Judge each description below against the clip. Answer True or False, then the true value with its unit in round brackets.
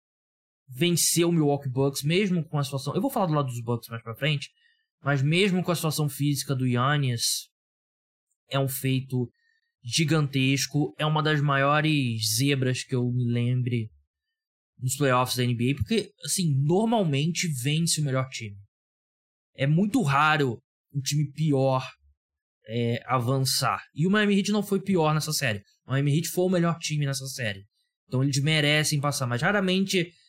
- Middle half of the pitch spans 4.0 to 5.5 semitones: True (4.3 semitones)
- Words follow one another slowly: False (160 wpm)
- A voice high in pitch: False (145 Hz)